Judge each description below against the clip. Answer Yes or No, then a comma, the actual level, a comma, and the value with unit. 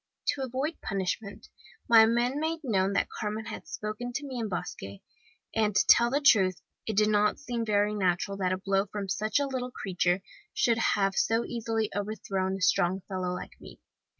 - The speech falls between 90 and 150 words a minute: No, average, 185 wpm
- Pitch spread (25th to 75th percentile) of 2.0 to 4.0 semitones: Yes, average, 3.5 semitones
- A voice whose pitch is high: Yes, high, 210 Hz